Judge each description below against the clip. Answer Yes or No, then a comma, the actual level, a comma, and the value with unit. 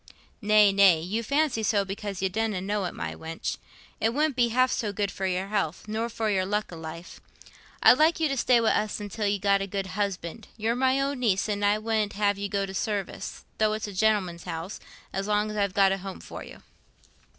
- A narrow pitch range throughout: Yes, narrow, 2.3 semitones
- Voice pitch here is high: Yes, high, 205 Hz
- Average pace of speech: No, fast, 230 wpm